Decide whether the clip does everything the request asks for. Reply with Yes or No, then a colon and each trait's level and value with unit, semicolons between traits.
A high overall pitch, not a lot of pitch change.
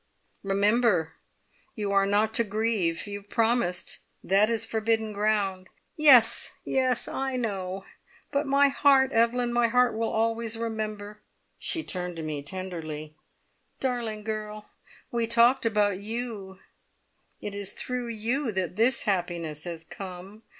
No: high, 215 Hz; average, 3.5 semitones